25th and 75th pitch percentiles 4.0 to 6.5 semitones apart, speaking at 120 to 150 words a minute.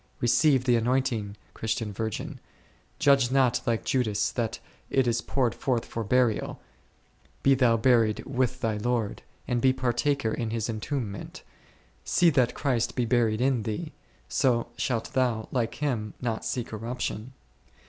No: narrow, 2.5 semitones; average, 145 wpm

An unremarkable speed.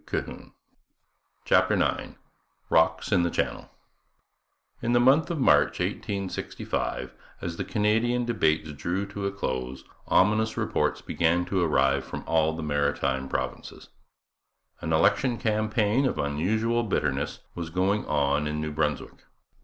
No: slow, 130 wpm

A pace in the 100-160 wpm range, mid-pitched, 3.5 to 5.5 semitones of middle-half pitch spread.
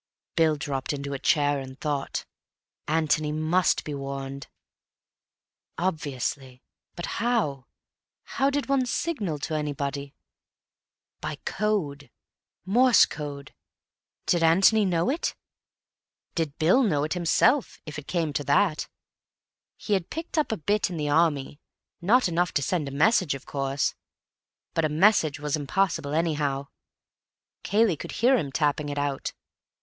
Yes: slow, 135 wpm; medium, 155 Hz; average, 5.1 semitones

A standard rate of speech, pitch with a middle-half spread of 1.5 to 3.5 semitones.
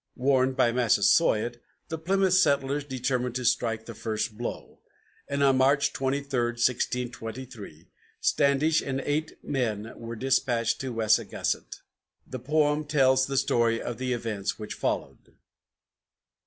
No: slow, 130 wpm; average, 3.2 semitones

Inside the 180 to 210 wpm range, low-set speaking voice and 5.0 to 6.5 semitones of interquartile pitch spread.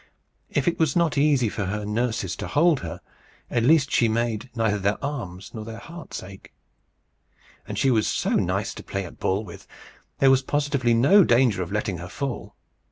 Yes: average, 190 wpm; low, 115 Hz; wide, 5.4 semitones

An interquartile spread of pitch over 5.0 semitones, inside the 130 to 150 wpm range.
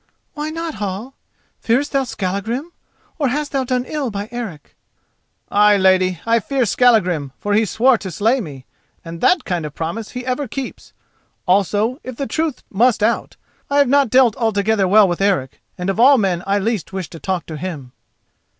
No: wide, 5.4 semitones; average, 185 wpm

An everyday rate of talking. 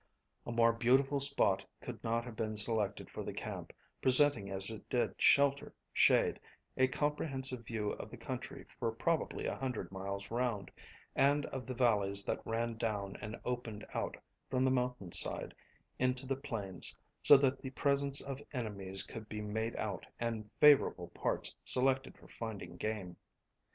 Yes: average, 160 wpm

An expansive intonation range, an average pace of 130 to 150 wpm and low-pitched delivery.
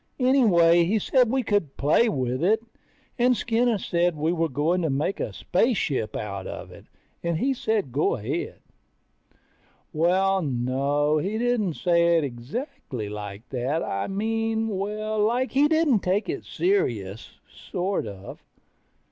No: wide, 8.3 semitones; average, 145 wpm; medium, 175 Hz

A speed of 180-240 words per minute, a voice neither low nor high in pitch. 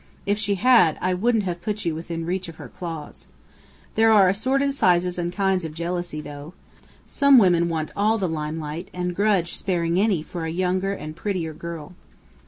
Yes: average, 190 wpm; medium, 180 Hz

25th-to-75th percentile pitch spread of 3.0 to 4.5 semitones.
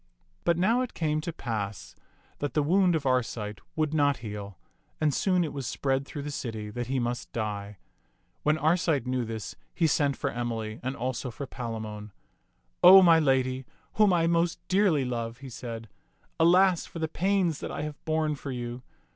No: wide, 5.6 semitones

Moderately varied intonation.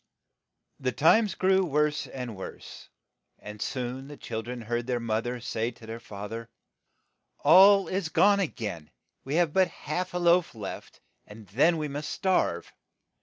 No: wide, 7.1 semitones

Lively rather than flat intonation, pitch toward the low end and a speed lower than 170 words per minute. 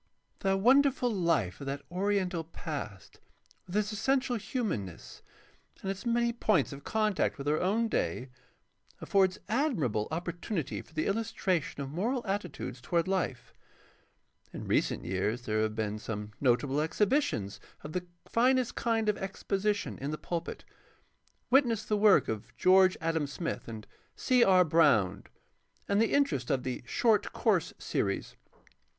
No: wide, 7.8 semitones; medium, 185 Hz; average, 145 wpm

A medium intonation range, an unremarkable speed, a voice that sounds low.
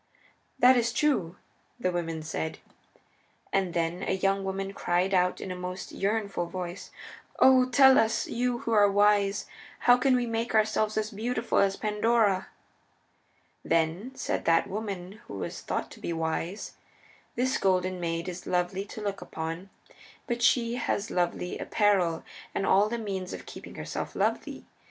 No: average, 3.9 semitones; average, 155 wpm; high, 195 Hz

